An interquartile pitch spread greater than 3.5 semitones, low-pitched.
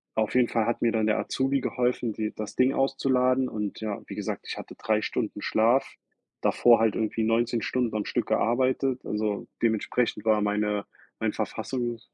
No: average, 2.8 semitones; low, 115 Hz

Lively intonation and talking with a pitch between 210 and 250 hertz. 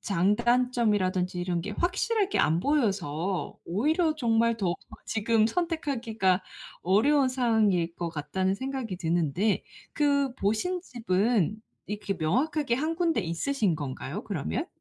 Yes: wide, 6.6 semitones; high, 215 Hz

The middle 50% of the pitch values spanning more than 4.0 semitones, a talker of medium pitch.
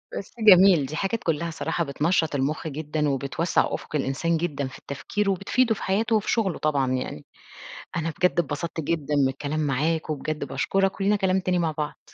Yes: average, 4.6 semitones; medium, 160 Hz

